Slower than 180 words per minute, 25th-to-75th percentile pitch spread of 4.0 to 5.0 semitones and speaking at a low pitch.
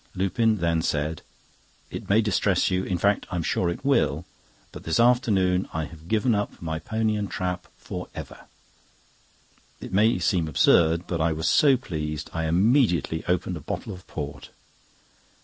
Yes: average, 155 wpm; average, 4.4 semitones; very low, 90 Hz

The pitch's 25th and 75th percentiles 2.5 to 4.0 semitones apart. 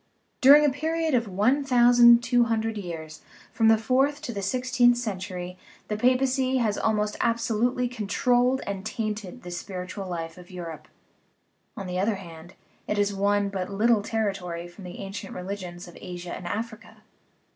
No: average, 4.8 semitones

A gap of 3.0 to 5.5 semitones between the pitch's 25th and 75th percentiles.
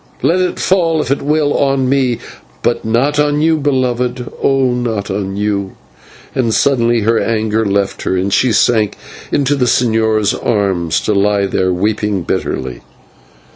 Yes: average, 5.0 semitones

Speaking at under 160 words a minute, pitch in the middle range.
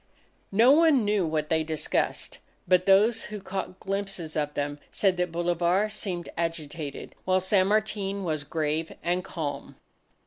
Yes: average, 145 wpm; medium, 180 Hz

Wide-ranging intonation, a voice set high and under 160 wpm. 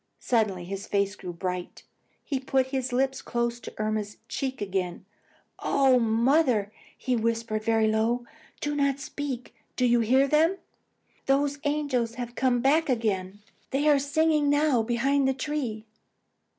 No: average, 4.2 semitones; high, 245 Hz; average, 145 wpm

